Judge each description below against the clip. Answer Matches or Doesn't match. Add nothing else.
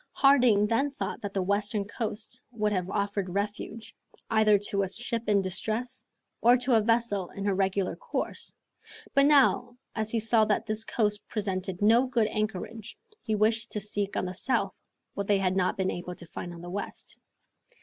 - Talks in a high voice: Matches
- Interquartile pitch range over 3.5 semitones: Doesn't match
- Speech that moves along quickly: Doesn't match